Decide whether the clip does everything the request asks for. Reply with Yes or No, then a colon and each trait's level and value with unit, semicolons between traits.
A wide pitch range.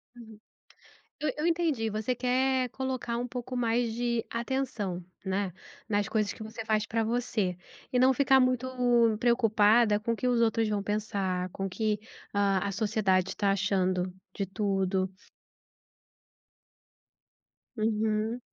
No: average, 3.3 semitones